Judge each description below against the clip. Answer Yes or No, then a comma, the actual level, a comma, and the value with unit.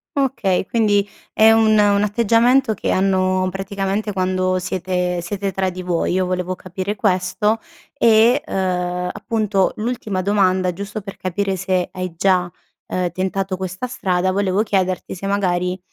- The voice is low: No, high, 190 Hz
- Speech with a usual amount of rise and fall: No, narrow, 2.0 semitones